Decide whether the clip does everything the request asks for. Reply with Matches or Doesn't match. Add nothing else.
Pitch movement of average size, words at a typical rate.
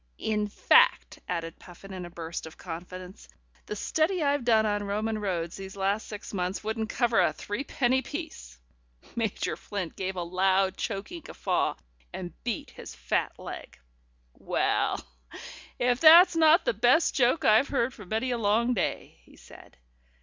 Matches